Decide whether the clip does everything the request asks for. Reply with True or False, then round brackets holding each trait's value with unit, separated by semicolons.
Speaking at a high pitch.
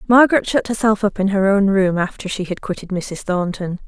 True (195 Hz)